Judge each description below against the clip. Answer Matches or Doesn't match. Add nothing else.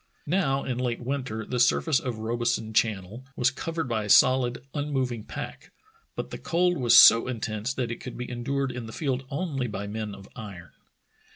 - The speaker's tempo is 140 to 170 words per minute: Doesn't match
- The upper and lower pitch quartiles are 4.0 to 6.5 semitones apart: Doesn't match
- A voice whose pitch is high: Doesn't match